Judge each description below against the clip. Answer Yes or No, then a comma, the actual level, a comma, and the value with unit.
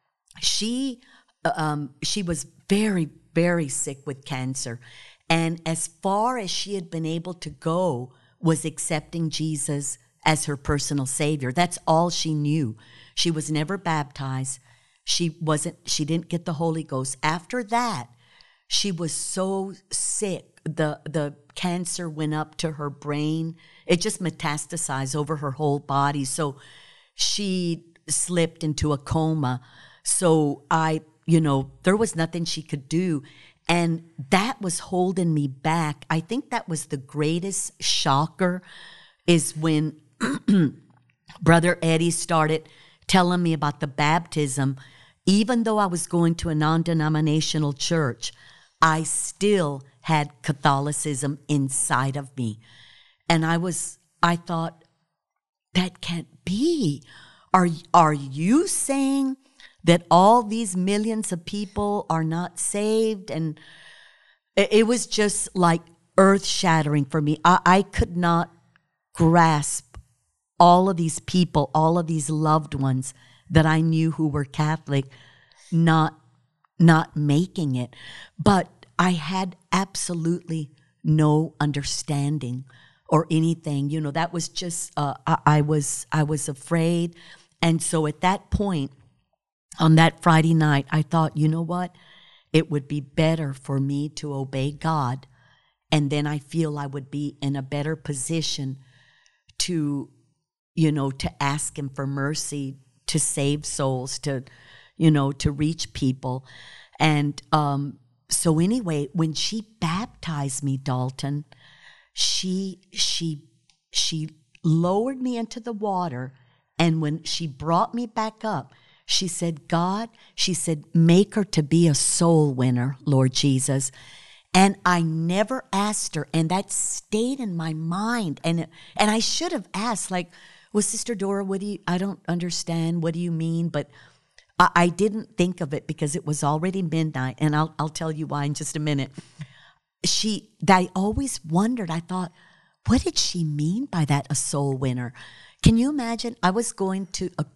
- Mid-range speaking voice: Yes, medium, 160 Hz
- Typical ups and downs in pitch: Yes, average, 3.4 semitones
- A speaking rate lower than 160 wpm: Yes, average, 145 wpm